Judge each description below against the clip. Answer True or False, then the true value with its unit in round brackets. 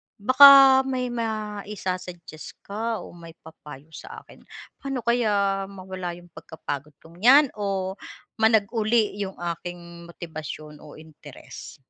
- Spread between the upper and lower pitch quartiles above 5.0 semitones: False (4.7 semitones)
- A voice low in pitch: False (190 Hz)